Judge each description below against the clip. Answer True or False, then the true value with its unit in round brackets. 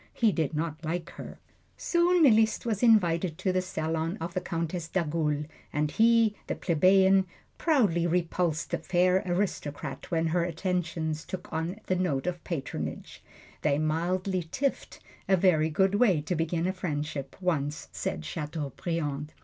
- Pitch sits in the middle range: True (170 Hz)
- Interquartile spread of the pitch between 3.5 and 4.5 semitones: False (3.0 semitones)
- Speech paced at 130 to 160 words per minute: True (150 wpm)